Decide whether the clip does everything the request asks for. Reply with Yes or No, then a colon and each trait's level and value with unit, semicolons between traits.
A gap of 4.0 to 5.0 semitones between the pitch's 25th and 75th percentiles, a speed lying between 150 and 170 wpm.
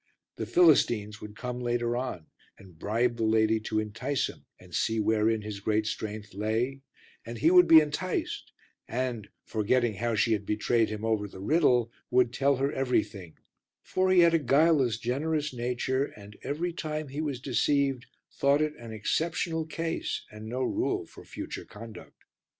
Yes: average, 4.7 semitones; average, 165 wpm